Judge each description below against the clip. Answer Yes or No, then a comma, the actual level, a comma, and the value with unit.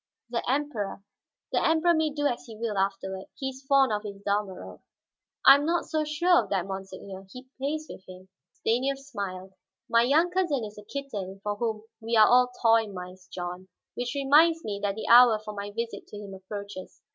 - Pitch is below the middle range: No, high, 225 Hz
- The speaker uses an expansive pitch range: Yes, wide, 5.8 semitones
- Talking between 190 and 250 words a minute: Yes, average, 200 wpm